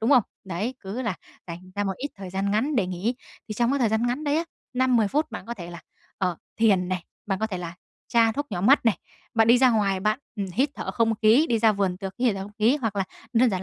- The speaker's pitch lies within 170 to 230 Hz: Yes, high, 220 Hz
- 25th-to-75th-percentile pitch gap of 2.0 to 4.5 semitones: Yes, average, 4.1 semitones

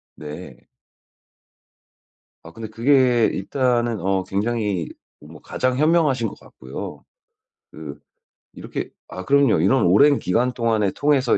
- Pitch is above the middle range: No, low, 115 Hz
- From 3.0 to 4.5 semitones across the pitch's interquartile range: No, wide, 5.5 semitones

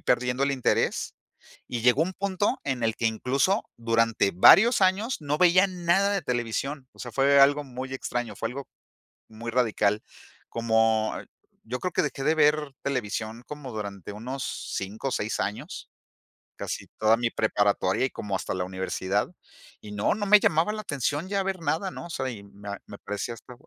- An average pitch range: No, wide, 5.8 semitones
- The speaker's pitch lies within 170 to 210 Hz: No, low, 125 Hz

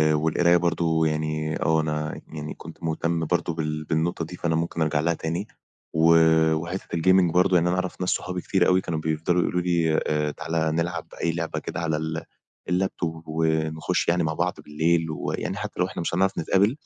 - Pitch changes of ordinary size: No, narrow, 1.8 semitones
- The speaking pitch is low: Yes, very low, 80 Hz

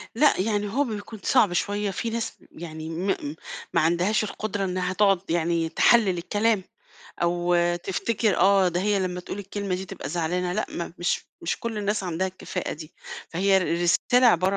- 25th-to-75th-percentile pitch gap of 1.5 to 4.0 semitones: Yes, average, 3.1 semitones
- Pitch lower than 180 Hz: No, high, 190 Hz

